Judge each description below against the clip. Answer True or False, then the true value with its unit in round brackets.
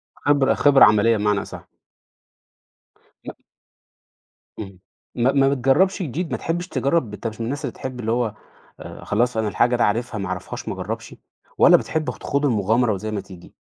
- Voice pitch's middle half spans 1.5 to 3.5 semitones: False (4.8 semitones)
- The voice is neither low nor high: False (120 Hz)